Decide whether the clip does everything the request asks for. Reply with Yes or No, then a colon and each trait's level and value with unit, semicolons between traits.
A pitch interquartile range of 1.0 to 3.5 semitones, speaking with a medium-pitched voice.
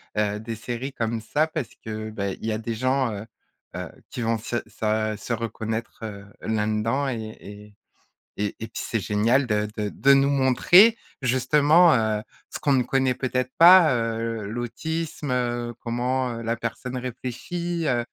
No: average, 3.2 semitones; low, 120 Hz